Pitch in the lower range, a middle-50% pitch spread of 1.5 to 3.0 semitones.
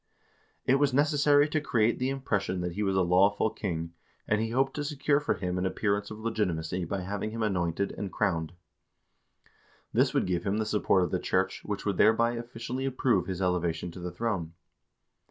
No: low, 100 Hz; average, 4.7 semitones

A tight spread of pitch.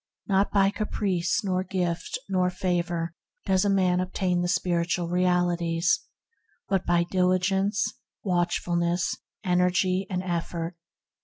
Yes: narrow, 1.4 semitones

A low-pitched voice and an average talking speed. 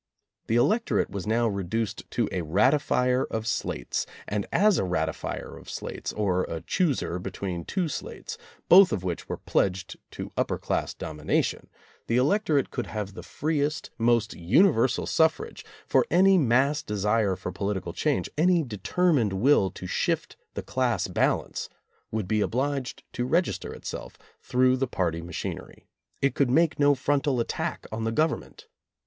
Yes: low, 120 Hz; average, 155 wpm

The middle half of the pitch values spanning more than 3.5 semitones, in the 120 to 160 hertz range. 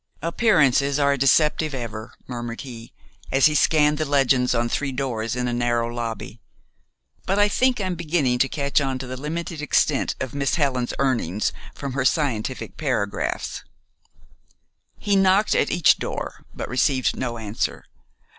Yes: average, 3.9 semitones; low, 135 Hz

